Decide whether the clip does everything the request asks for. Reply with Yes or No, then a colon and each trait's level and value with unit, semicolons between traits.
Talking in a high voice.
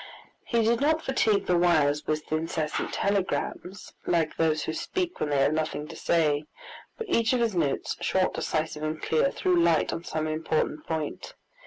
No: medium, 165 Hz